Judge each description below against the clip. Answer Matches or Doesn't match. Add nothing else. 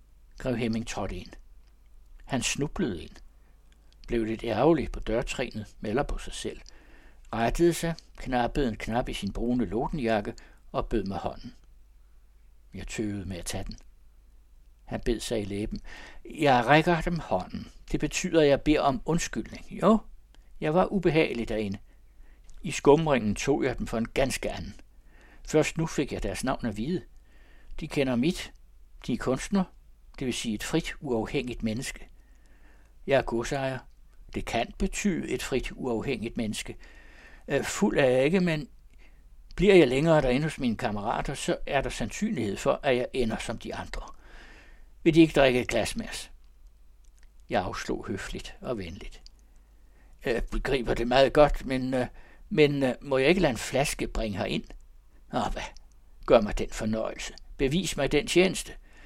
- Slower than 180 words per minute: Matches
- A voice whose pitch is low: Matches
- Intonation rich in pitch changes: Matches